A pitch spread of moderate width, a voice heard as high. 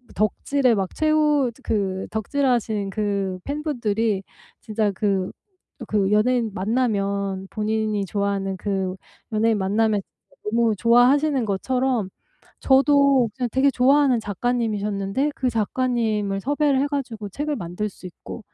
Yes: average, 4.5 semitones; high, 220 Hz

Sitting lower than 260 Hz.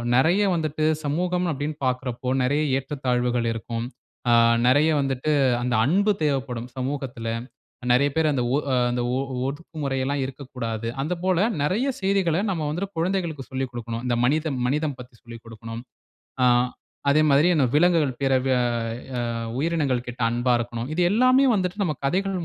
Yes: medium, 140 Hz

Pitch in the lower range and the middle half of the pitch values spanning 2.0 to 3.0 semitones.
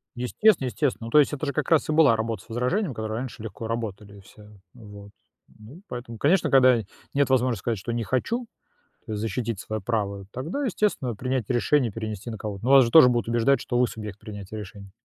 No: low, 120 Hz; average, 3.6 semitones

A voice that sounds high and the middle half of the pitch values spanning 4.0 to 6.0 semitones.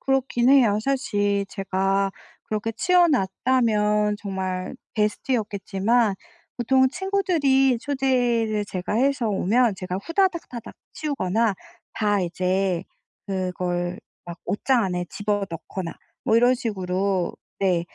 Yes: high, 210 Hz; average, 5.2 semitones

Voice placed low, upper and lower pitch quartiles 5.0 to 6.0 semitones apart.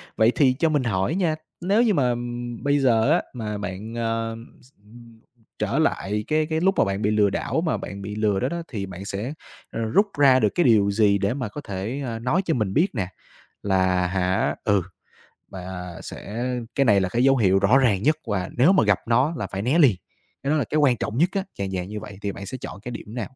Yes: low, 115 Hz; wide, 5.5 semitones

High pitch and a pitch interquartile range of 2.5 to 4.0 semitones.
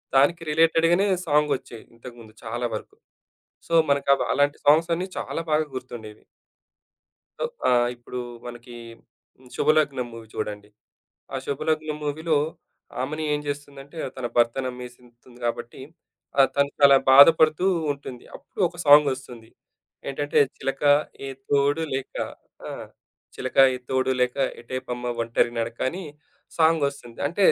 No: low, 135 Hz; average, 3.7 semitones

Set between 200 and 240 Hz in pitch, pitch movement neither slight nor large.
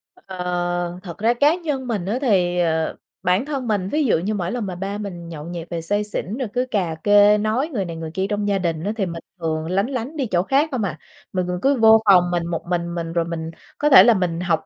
No: high, 190 Hz; average, 4.4 semitones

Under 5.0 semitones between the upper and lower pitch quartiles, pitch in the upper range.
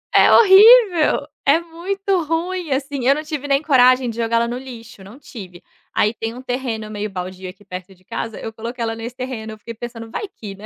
No: wide, 5.4 semitones; high, 245 Hz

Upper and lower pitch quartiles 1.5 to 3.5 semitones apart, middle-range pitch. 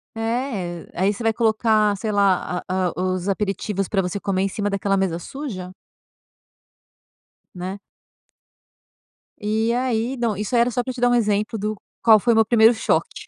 No: average, 3.1 semitones; high, 210 Hz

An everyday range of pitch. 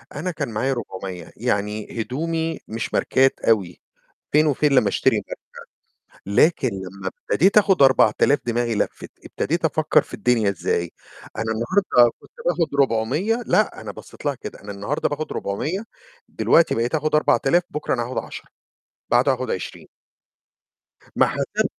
No: wide, 6.1 semitones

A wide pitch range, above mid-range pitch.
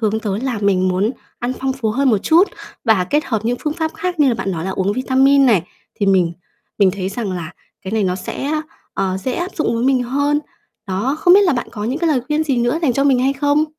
Yes: wide, 6.1 semitones; high, 245 Hz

